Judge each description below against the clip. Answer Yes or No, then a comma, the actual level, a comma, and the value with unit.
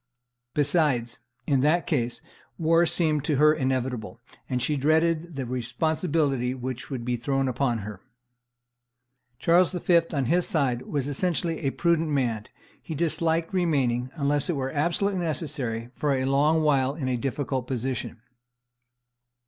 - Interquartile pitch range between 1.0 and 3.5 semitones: No, average, 4.1 semitones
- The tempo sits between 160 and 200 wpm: No, average, 140 wpm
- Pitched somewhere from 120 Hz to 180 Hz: Yes, medium, 140 Hz